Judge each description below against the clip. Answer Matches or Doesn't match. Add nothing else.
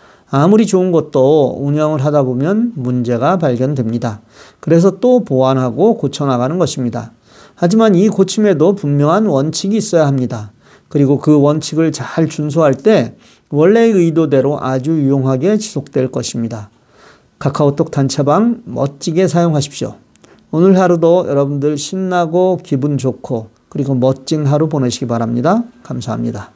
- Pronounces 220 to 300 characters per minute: Doesn't match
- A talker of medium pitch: Matches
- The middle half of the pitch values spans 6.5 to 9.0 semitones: Doesn't match